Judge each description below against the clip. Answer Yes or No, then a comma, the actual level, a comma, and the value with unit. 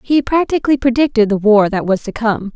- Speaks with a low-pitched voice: No, high, 235 Hz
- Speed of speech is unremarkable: No, fast, 210 wpm